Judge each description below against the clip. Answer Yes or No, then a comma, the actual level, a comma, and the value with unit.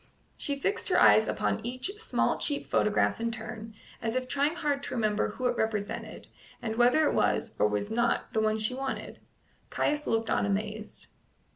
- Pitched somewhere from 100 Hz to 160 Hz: No, high, 230 Hz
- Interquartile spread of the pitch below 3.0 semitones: No, average, 3.8 semitones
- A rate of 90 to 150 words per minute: No, average, 180 wpm